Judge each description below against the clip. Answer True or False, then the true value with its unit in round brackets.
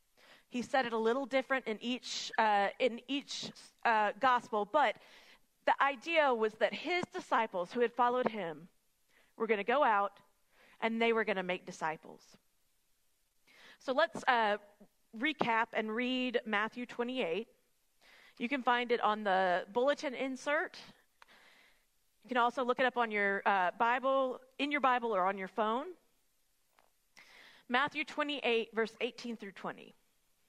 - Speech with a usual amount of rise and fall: True (3.3 semitones)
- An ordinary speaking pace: True (150 wpm)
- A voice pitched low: False (235 Hz)